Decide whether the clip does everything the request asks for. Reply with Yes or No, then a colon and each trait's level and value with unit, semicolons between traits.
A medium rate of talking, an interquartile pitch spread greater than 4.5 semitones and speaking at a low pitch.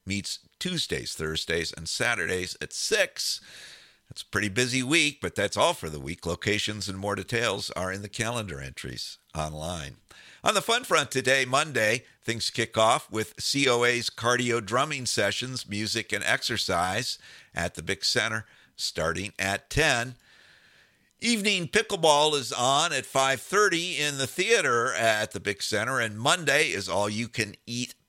Yes: average, 155 wpm; wide, 5.5 semitones; low, 115 Hz